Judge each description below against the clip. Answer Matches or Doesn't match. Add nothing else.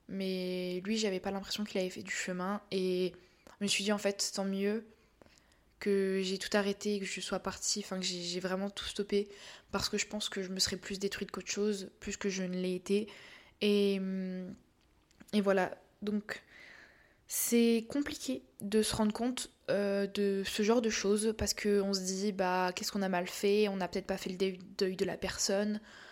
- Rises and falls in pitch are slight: Matches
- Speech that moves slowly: Doesn't match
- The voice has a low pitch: Doesn't match